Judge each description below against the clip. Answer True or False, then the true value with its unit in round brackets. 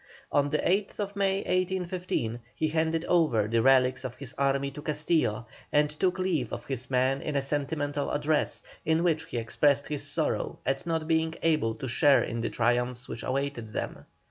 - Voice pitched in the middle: True (145 Hz)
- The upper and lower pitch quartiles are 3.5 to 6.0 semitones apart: True (4.2 semitones)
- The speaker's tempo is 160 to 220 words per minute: True (180 wpm)